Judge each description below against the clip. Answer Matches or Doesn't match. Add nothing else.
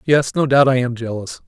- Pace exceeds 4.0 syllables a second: Matches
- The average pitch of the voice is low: Matches